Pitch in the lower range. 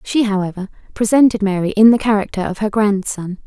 No: high, 205 Hz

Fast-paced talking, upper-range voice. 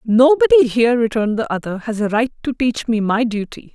Yes: fast, 210 wpm; high, 235 Hz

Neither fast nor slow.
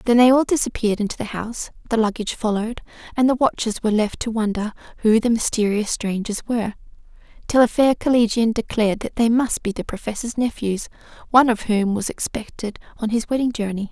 Yes: average, 185 wpm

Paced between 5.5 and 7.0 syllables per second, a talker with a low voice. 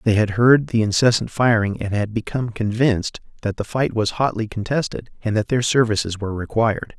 Yes: 5.7 syllables/s; low, 110 Hz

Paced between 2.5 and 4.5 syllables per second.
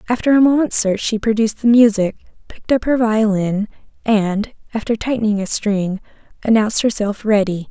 No: 5.5 syllables/s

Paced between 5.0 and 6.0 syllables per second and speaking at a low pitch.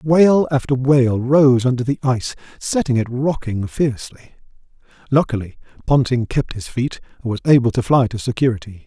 Yes: 5.4 syllables/s; low, 130 Hz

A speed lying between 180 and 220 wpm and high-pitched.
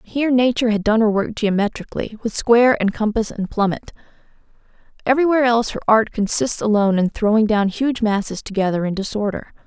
No: average, 170 wpm; high, 220 Hz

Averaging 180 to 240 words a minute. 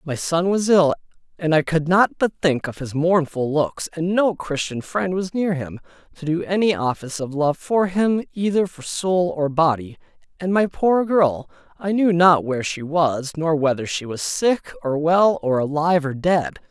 Yes: average, 200 wpm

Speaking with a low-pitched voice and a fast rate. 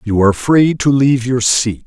Yes: low, 125 Hz; fast, 225 wpm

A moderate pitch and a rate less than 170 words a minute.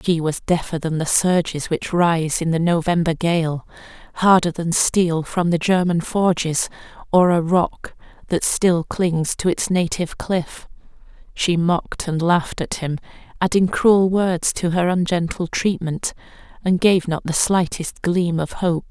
Yes: medium, 170 Hz; average, 160 wpm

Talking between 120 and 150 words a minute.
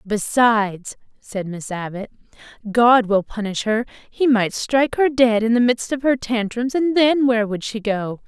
No: average, 180 wpm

